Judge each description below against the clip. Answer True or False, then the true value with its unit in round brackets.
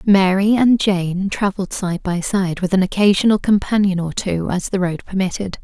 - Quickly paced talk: False (180 wpm)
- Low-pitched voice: False (190 Hz)